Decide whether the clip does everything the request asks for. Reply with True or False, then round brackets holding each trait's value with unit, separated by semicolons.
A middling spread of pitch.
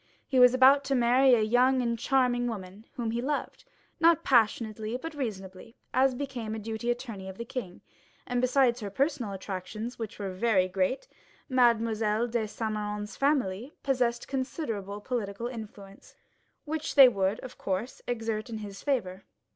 True (3.6 semitones)